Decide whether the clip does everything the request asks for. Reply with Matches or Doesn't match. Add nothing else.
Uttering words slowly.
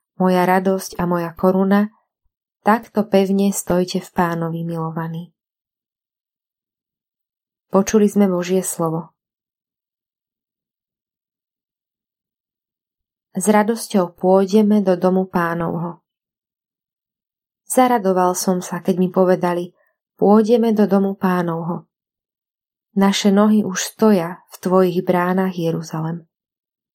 Matches